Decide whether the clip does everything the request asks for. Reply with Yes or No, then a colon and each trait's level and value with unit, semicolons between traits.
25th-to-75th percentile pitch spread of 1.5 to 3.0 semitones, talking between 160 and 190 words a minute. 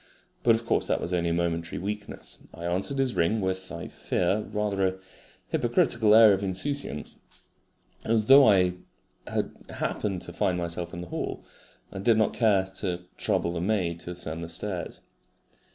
No: average, 3.7 semitones; average, 170 wpm